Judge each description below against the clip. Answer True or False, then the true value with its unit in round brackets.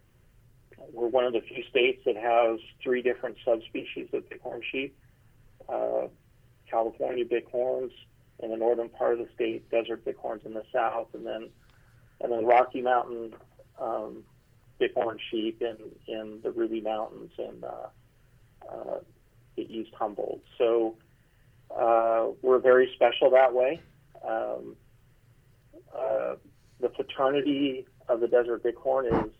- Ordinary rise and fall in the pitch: False (2.0 semitones)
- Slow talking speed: True (130 wpm)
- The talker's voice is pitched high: False (120 Hz)